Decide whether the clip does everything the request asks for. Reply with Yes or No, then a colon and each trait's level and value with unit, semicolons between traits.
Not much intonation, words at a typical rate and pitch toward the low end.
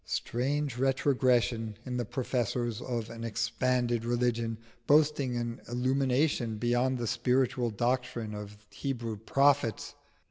No: narrow, 2.1 semitones; slow, 110 wpm; low, 120 Hz